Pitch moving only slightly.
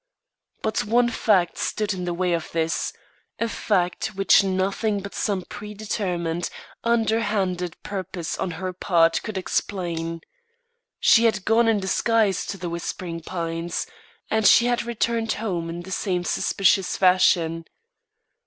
No: average, 3.8 semitones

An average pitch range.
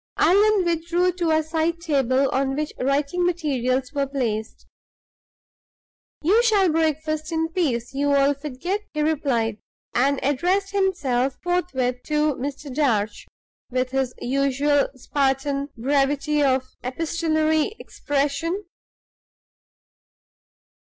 Yes: average, 3.7 semitones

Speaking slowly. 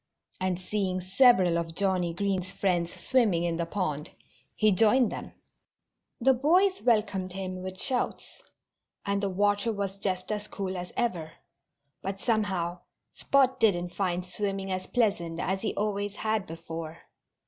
No: average, 145 wpm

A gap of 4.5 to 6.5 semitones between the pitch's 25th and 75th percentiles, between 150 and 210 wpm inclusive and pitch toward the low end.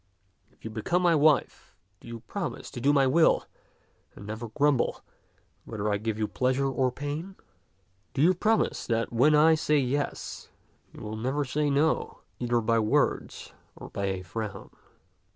Yes: average, 5.0 semitones; average, 165 wpm; low, 130 Hz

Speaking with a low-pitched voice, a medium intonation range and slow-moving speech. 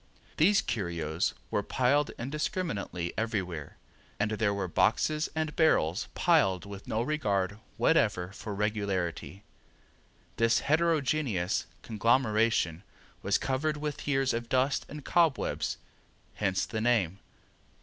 No: low, 110 Hz; wide, 7.0 semitones; slow, 110 wpm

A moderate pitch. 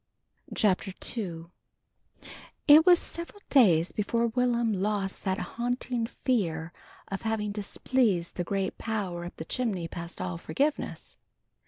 No: high, 210 Hz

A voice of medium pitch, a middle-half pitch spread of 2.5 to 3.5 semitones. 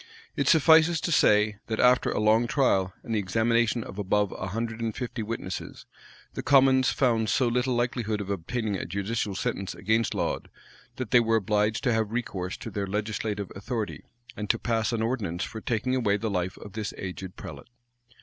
No: low, 110 Hz; average, 2.9 semitones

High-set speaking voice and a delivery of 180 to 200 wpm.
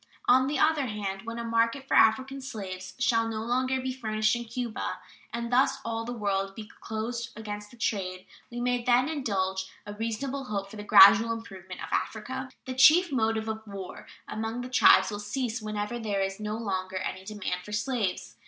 Yes: high, 225 Hz; average, 190 wpm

